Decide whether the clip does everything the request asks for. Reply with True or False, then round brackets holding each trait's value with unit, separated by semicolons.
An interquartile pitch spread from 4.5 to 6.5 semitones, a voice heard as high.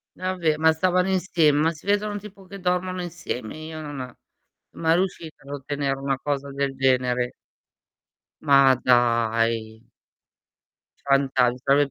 False (5.1 semitones; 145 Hz)